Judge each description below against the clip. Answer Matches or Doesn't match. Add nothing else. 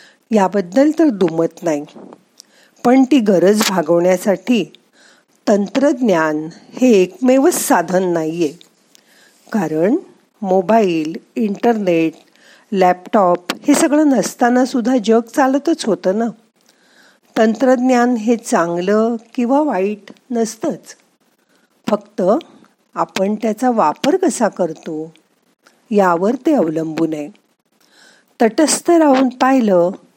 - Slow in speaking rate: Doesn't match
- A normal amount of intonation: Doesn't match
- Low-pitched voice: Doesn't match